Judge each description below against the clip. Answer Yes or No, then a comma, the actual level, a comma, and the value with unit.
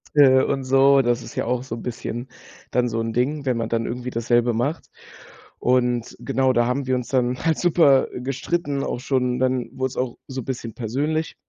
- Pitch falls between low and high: No, low, 125 Hz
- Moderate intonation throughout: No, narrow, 2.0 semitones